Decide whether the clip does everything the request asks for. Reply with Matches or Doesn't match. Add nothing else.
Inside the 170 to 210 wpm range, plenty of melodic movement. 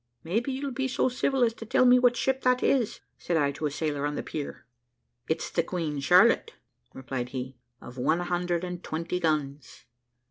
Matches